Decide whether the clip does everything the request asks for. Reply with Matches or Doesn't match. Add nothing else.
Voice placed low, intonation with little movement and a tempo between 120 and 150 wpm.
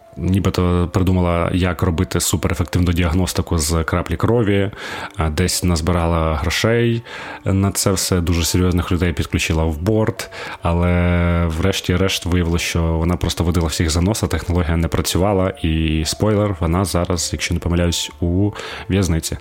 Matches